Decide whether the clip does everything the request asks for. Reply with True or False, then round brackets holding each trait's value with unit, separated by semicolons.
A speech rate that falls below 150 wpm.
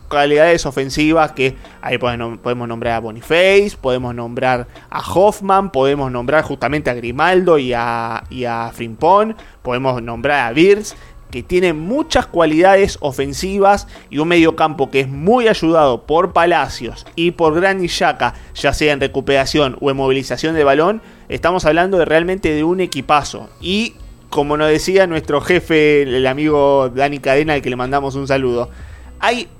False (160 wpm)